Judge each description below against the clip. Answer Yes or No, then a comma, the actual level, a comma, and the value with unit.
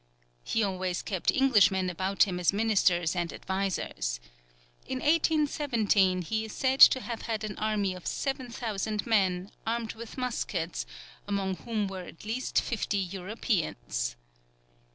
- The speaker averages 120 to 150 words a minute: Yes, slow, 135 wpm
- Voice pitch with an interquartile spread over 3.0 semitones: Yes, average, 3.8 semitones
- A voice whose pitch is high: Yes, high, 205 Hz